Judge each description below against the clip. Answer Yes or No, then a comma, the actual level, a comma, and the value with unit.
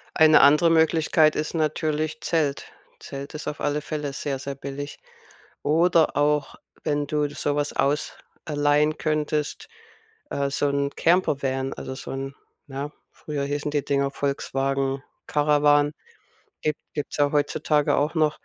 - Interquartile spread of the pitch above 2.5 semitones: No, narrow, 1.4 semitones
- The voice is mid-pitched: Yes, medium, 145 Hz